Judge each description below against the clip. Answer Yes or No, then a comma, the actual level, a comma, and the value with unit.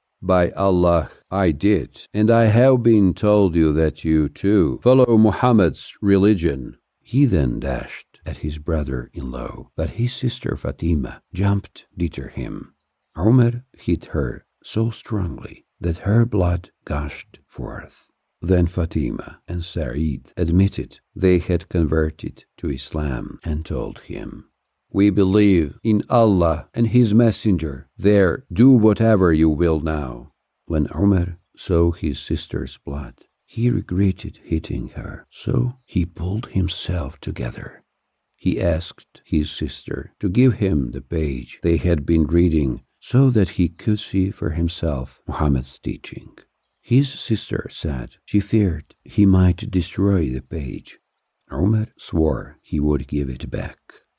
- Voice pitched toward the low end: Yes, very low, 90 Hz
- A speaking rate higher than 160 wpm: No, slow, 135 wpm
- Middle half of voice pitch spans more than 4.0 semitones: Yes, average, 5.2 semitones